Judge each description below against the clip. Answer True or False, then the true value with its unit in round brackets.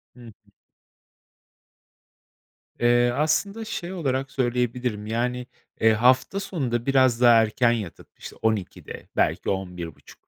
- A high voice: False (120 Hz)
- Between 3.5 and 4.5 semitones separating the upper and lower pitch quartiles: False (3.1 semitones)